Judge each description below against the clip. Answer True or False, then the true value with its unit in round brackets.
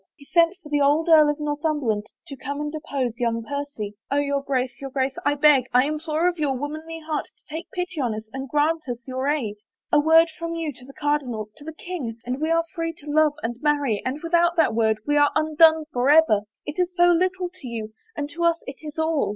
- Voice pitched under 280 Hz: False (295 Hz)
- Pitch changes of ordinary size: True (3.5 semitones)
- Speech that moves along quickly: True (235 wpm)